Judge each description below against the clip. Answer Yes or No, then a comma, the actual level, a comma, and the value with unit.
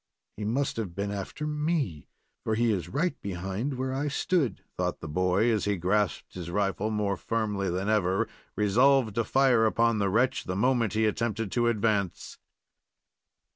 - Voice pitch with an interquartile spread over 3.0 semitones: Yes, average, 3.8 semitones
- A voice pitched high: No, low, 110 Hz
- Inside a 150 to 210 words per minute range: Yes, average, 170 wpm